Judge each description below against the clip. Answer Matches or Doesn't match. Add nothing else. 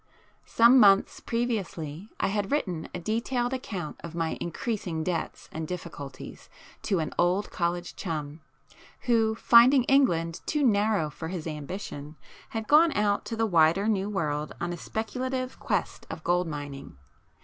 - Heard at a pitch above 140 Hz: Matches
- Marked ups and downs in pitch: Matches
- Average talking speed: Matches